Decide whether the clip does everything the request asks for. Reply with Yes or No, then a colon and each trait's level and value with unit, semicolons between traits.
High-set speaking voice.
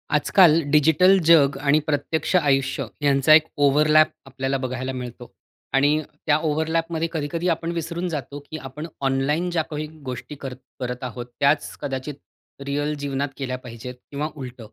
No: medium, 145 Hz